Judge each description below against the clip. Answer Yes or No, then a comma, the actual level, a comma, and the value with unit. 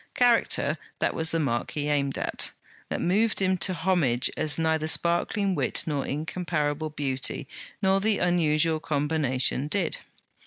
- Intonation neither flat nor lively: Yes, average, 3.5 semitones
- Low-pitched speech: No, medium, 160 Hz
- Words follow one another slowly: No, average, 145 wpm